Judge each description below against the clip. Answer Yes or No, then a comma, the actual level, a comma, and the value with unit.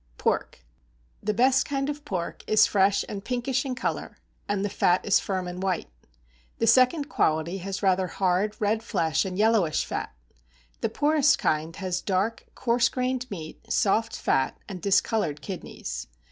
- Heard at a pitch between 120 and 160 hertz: No, high, 200 Hz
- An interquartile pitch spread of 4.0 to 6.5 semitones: Yes, average, 5.1 semitones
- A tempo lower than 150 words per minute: No, average, 160 wpm